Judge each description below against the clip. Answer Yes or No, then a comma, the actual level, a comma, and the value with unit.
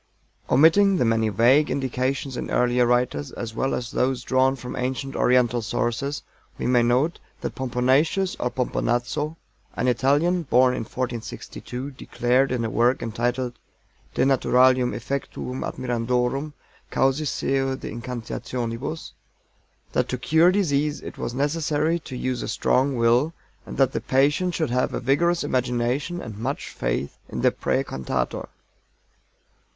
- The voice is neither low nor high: No, low, 130 Hz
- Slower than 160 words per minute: Yes, average, 140 wpm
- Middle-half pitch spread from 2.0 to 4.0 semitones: Yes, narrow, 2.6 semitones